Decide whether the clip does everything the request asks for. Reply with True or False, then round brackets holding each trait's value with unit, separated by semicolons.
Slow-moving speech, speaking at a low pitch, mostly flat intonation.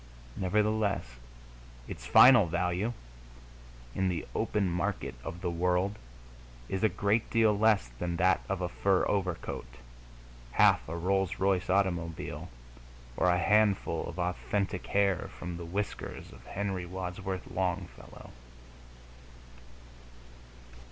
True (115 wpm; 95 Hz; 2.3 semitones)